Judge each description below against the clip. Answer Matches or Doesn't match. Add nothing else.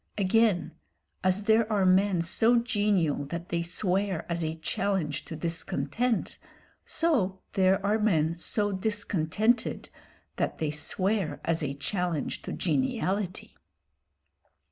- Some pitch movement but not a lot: Matches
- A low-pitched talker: Doesn't match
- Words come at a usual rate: Doesn't match